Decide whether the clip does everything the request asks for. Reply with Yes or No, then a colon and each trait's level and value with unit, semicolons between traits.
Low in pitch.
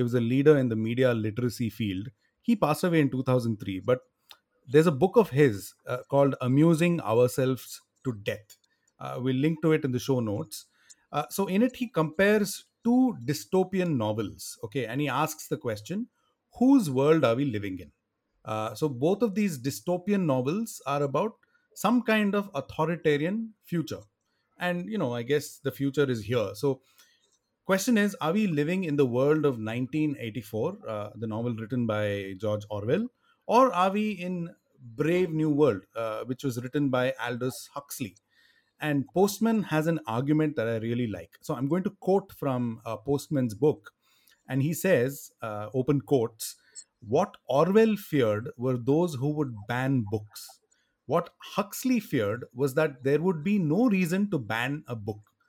No: medium, 145 Hz